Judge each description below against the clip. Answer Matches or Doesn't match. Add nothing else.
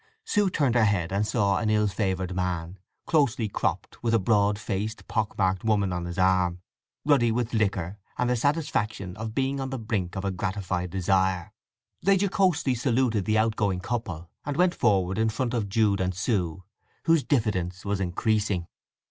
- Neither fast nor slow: Matches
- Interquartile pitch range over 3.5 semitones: Matches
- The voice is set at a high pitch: Doesn't match